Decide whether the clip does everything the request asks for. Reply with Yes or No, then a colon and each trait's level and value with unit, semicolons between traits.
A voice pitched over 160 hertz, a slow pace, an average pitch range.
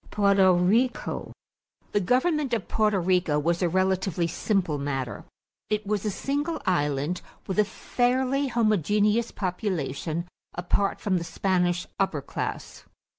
Yes: high, 190 Hz; slow, 125 wpm; average, 3.7 semitones